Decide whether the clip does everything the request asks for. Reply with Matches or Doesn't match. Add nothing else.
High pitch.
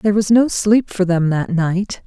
Matches